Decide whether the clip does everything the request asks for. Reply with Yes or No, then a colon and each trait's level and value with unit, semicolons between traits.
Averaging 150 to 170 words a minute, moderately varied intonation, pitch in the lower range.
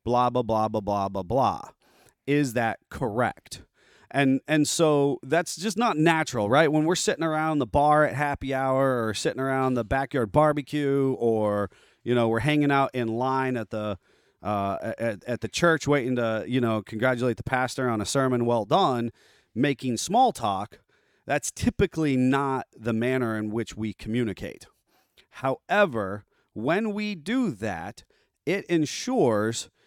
Yes: average, 160 wpm; average, 4.6 semitones; low, 130 Hz